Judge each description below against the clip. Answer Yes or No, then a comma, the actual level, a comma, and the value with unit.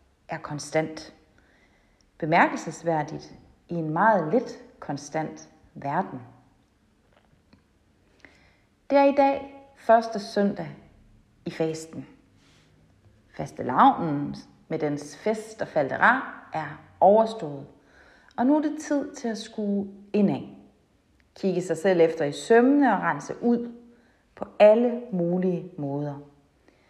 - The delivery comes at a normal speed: No, slow, 105 wpm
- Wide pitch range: Yes, wide, 7.2 semitones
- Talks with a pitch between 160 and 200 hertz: Yes, high, 190 Hz